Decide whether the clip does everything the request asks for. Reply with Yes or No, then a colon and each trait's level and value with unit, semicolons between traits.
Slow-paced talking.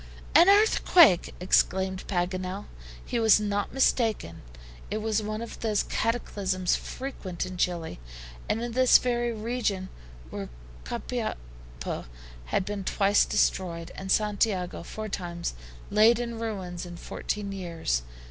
Yes: slow, 125 wpm